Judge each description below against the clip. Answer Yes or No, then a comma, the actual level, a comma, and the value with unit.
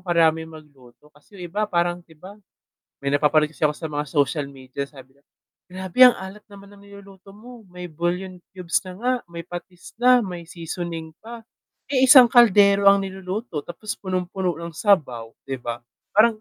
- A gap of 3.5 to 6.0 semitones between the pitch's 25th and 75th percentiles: Yes, average, 4.4 semitones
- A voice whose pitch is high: No, medium, 180 Hz